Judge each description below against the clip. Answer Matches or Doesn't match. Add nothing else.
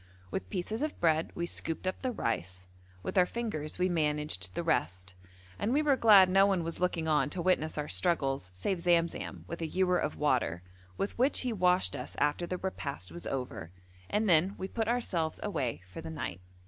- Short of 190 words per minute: Doesn't match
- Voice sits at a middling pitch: Matches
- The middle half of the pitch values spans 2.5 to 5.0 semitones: Doesn't match